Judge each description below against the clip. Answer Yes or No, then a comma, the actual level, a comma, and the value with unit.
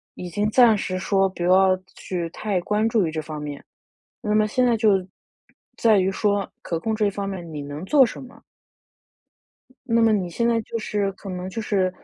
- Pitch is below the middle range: No, high, 200 Hz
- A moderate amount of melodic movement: Yes, average, 3.2 semitones